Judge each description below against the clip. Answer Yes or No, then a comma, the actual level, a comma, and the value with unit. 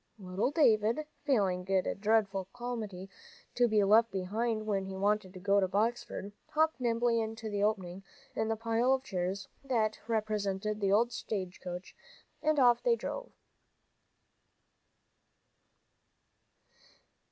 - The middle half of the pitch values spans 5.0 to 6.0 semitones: No, average, 3.4 semitones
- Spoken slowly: Yes, slow, 130 wpm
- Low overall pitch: No, high, 215 Hz